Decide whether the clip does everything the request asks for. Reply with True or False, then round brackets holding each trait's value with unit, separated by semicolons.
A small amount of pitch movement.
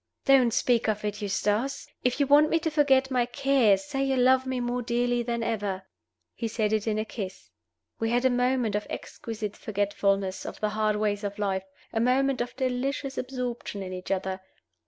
False (3.9 semitones)